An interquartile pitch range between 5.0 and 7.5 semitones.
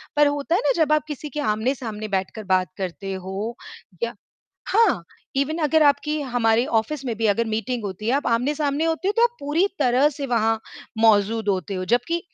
Yes: wide, 5.6 semitones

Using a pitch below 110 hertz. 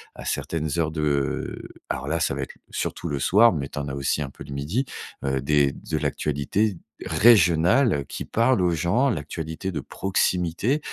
Yes: very low, 80 Hz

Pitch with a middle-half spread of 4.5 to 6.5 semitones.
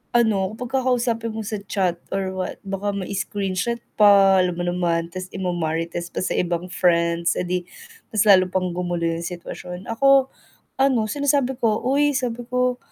Yes: average, 4.9 semitones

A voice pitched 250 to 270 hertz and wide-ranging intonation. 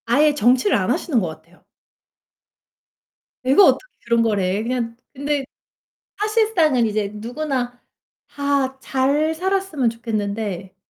No: very high, 255 Hz; average, 5.0 semitones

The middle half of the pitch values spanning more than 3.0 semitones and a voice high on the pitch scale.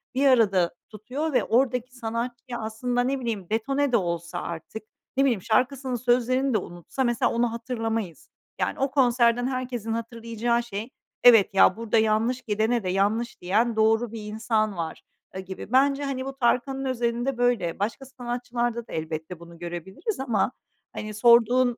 No: average, 2.7 semitones; high, 235 Hz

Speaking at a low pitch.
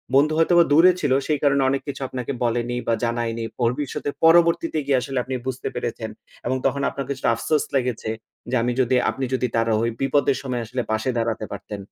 Yes: low, 130 Hz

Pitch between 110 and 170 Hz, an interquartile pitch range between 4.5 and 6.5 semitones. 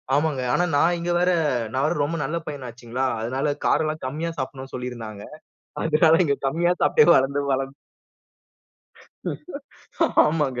No: medium, 140 Hz; average, 3.6 semitones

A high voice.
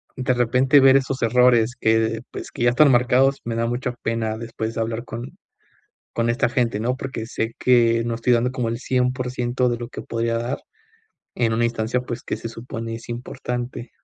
No: low, 120 Hz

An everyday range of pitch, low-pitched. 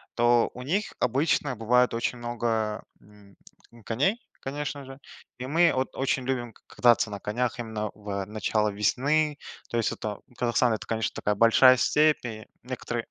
Yes: average, 3.3 semitones; low, 120 Hz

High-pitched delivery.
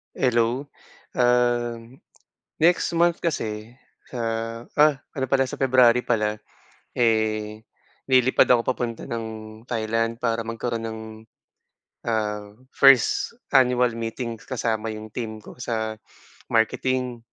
No: low, 115 Hz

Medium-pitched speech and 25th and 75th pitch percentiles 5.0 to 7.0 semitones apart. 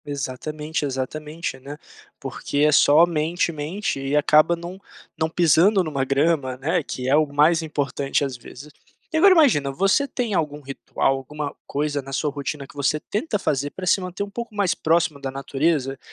No: medium, 150 Hz; average, 3.5 semitones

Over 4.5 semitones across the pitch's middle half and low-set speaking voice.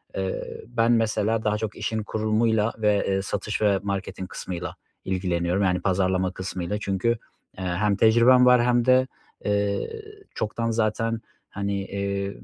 No: average, 2.8 semitones; low, 105 Hz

